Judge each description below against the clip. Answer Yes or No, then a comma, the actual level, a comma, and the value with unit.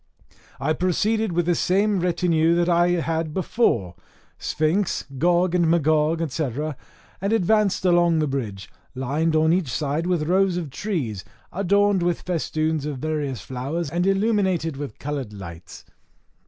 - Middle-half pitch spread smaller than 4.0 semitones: Yes, average, 3.5 semitones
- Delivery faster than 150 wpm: No, average, 140 wpm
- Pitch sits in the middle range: Yes, medium, 165 Hz